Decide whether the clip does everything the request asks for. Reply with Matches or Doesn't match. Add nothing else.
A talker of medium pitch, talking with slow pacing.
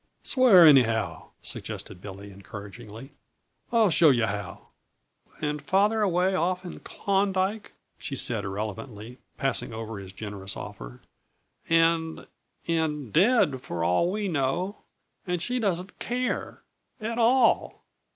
Matches